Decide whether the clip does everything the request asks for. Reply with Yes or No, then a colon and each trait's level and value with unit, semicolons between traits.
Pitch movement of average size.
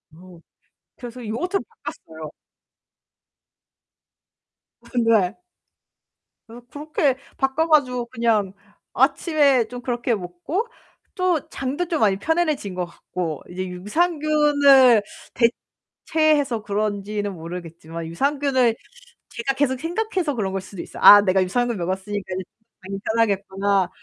No: wide, 6.9 semitones